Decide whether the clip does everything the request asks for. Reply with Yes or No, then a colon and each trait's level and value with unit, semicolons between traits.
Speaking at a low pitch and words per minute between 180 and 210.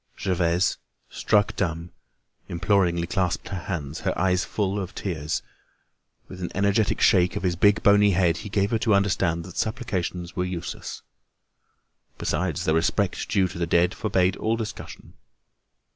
No: very low, 95 Hz; average, 150 wpm